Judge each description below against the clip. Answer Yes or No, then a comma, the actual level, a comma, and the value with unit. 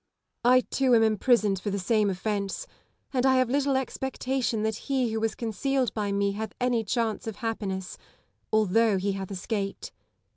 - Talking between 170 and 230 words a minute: Yes, average, 175 wpm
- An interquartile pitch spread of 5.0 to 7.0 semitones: No, average, 3.9 semitones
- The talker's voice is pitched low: No, high, 220 Hz